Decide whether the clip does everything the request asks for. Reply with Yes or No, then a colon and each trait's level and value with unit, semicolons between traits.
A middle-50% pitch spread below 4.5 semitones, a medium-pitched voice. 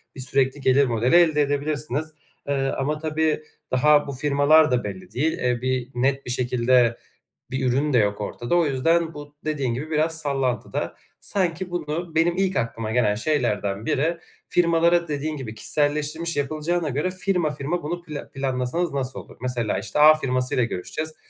Yes: average, 3.9 semitones; medium, 145 Hz